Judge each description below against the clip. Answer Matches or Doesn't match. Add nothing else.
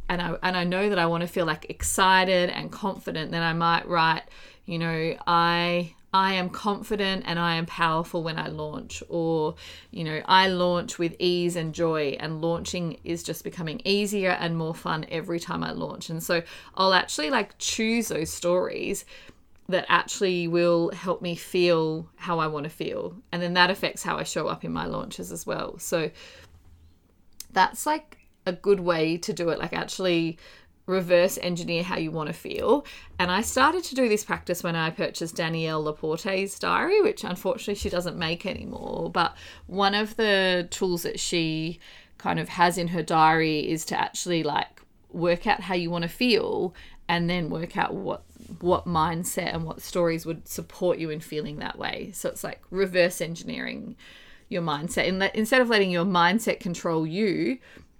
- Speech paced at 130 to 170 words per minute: Doesn't match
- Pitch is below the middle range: Doesn't match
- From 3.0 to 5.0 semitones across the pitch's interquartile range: Doesn't match